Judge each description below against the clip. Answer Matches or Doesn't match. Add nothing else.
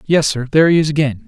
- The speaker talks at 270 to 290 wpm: Doesn't match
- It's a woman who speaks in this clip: Doesn't match